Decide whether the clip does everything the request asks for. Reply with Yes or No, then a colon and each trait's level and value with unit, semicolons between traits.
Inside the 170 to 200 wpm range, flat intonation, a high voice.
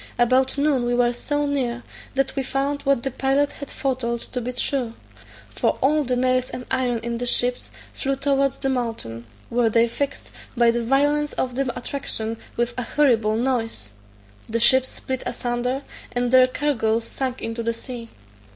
Yes: average, 175 wpm; narrow, 2.3 semitones; very high, 250 Hz